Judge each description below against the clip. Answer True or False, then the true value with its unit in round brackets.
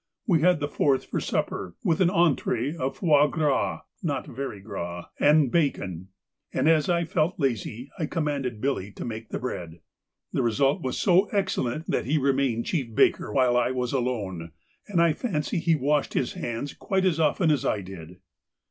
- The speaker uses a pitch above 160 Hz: False (140 Hz)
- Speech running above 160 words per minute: True (180 wpm)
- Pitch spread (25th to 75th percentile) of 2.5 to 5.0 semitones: False (5.5 semitones)